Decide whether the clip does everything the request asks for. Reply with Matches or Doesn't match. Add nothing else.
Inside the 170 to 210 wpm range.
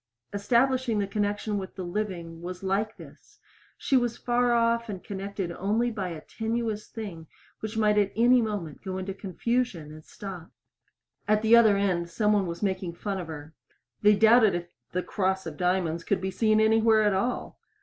Matches